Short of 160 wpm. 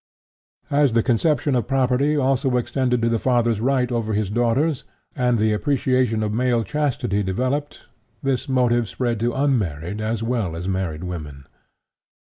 Yes: average, 150 wpm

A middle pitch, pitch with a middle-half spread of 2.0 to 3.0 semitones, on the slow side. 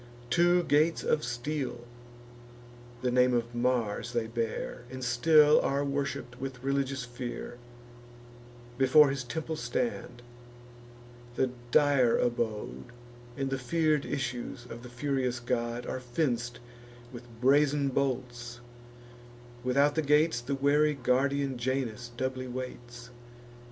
No: low, 130 Hz; average, 2.7 semitones; slow, 115 wpm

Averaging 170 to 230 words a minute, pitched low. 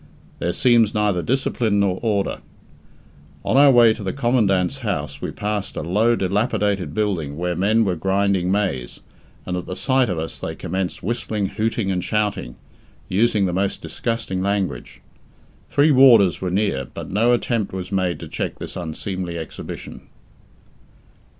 No: average, 155 wpm; low, 100 Hz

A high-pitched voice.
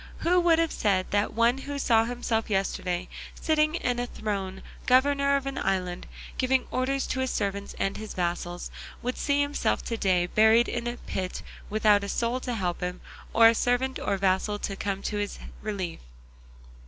Yes: high, 220 Hz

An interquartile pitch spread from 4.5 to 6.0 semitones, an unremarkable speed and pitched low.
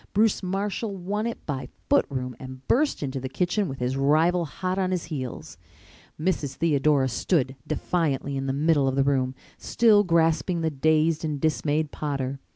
No: average, 4.9 semitones; average, 170 wpm; medium, 155 Hz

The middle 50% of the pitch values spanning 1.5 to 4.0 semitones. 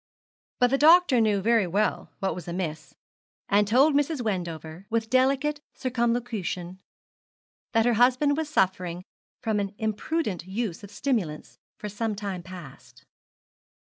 No: average, 5.3 semitones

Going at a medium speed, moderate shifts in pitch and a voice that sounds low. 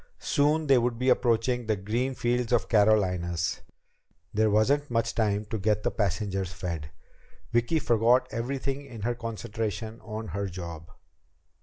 Yes: average, 150 wpm; average, 3.3 semitones; low, 115 Hz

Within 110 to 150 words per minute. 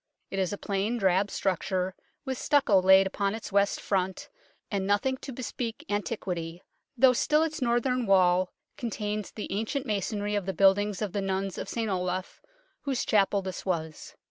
No: average, 170 wpm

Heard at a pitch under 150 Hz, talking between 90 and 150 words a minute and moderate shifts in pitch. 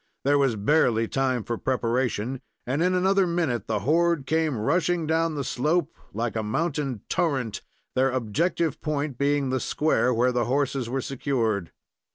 No: low, 135 Hz; average, 160 wpm; average, 4.8 semitones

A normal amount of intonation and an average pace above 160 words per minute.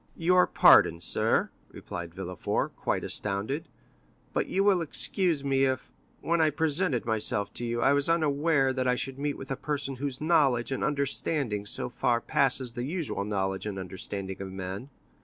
No: wide, 5.9 semitones; average, 170 wpm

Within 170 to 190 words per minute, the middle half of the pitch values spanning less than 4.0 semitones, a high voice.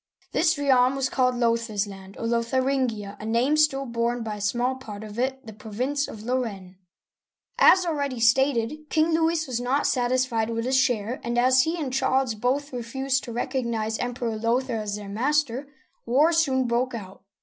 Yes: average, 175 wpm; average, 2.8 semitones; high, 245 Hz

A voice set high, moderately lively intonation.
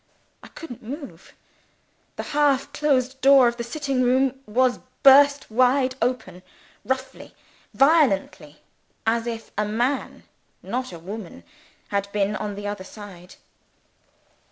Yes: very high, 250 Hz; average, 4.5 semitones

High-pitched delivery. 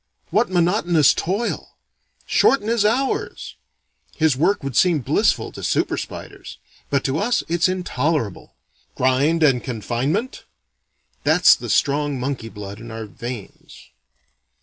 No: medium, 150 Hz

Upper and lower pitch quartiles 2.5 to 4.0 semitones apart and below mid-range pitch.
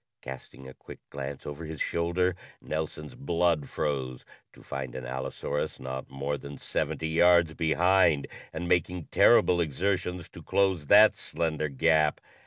Yes: average, 3.7 semitones; very low, 80 Hz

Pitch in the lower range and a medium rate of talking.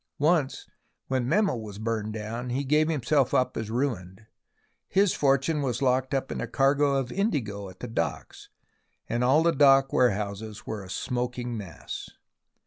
Yes: low, 125 Hz; average, 160 wpm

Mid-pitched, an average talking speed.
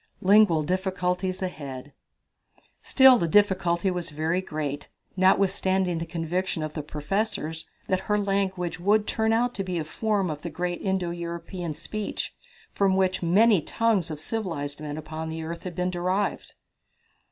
Yes: medium, 180 Hz; average, 155 wpm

